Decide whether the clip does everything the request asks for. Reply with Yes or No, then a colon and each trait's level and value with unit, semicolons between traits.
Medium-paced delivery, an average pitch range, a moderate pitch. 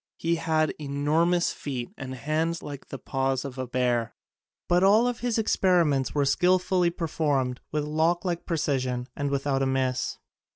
Yes: average, 170 wpm; average, 4.3 semitones; medium, 150 Hz